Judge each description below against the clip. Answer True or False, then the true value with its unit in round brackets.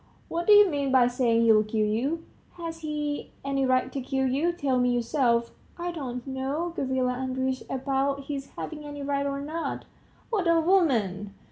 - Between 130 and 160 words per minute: False (175 wpm)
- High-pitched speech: True (275 Hz)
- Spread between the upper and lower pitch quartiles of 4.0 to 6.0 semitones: False (3.5 semitones)